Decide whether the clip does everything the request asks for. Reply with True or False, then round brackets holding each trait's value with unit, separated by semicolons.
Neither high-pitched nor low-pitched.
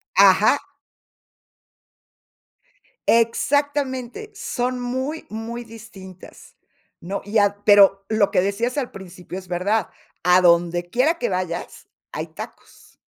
False (215 Hz)